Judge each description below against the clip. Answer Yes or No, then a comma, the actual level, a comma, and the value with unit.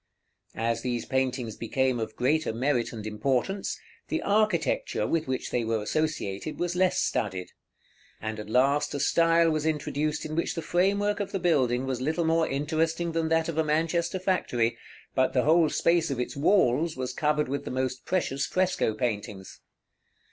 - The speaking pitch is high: No, medium, 145 Hz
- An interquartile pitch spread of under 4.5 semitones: No, average, 5.1 semitones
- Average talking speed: Yes, average, 170 wpm